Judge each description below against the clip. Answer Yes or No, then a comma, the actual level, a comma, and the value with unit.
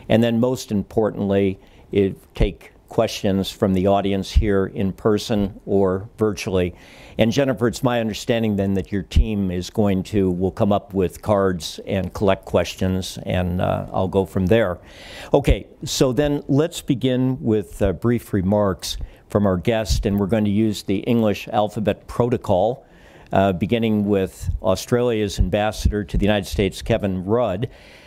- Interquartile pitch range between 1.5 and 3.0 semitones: Yes, average, 2.7 semitones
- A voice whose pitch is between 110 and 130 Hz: No, low, 100 Hz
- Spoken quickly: No, average, 155 wpm